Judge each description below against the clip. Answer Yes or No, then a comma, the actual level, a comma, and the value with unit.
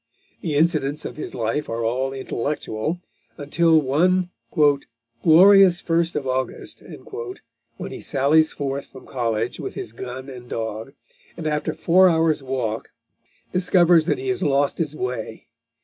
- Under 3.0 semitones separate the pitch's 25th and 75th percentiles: No, average, 4.6 semitones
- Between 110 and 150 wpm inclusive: Yes, average, 140 wpm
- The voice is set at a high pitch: No, medium, 145 Hz